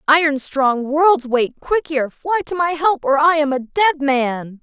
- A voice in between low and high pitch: No, very high, 295 Hz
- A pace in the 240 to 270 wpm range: No, fast, 205 wpm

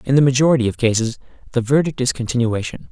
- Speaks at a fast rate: No, average, 185 wpm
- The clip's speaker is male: Yes, male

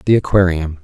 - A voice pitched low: Yes, very low, 90 Hz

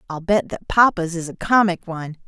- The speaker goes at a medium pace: No, fast, 210 wpm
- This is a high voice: No, medium, 180 Hz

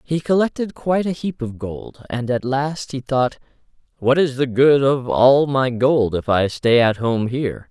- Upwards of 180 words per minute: Yes, average, 200 wpm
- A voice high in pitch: No, low, 135 Hz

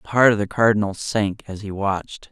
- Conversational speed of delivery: No, fast, 235 wpm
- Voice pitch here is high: No, low, 105 Hz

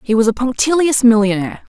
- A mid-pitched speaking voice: No, high, 235 Hz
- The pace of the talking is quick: No, average, 170 wpm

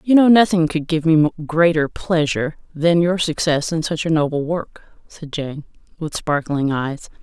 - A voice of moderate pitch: Yes, medium, 160 Hz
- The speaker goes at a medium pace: Yes, average, 175 wpm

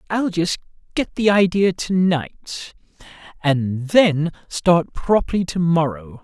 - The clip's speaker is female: No, male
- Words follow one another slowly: Yes, slow, 125 wpm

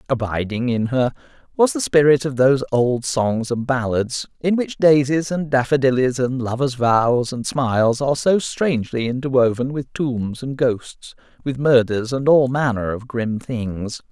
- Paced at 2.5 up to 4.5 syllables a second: Yes, 4.4 syllables/s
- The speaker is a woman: No, male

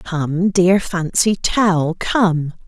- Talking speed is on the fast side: No, slow, 110 wpm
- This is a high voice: No, medium, 175 Hz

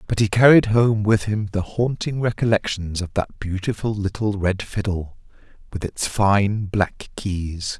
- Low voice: Yes, low, 100 Hz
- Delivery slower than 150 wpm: No, average, 155 wpm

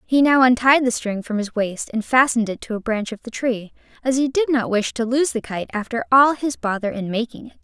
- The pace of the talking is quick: Yes, fast, 260 wpm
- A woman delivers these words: Yes, female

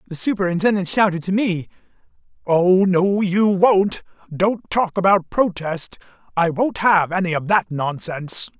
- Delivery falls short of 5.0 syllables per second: Yes, 4.4 syllables/s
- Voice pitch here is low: No, medium, 185 Hz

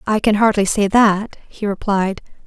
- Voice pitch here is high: Yes, high, 205 Hz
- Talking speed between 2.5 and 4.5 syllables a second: Yes, 4.4 syllables/s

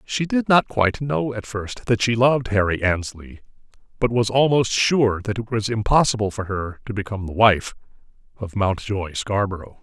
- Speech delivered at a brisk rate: No, average, 175 wpm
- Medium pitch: No, low, 105 Hz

